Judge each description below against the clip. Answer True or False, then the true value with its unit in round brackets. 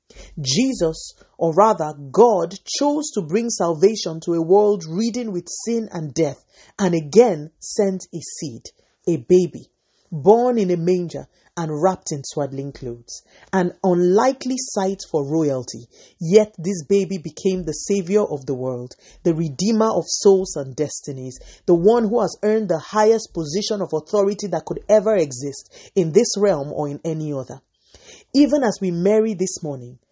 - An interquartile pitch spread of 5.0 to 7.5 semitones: True (5.3 semitones)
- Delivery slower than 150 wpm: False (155 wpm)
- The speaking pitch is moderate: True (180 Hz)